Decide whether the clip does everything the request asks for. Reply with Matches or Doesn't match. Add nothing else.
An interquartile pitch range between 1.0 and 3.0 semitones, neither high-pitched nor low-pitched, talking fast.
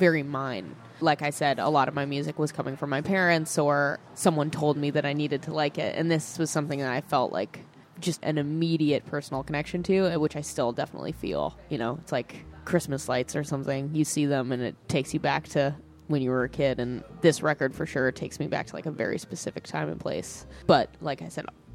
Matches